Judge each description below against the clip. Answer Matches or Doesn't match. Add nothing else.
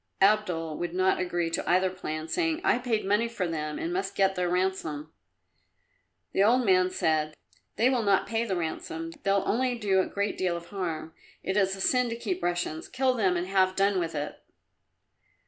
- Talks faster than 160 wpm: Matches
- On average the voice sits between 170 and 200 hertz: Matches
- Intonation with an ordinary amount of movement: Matches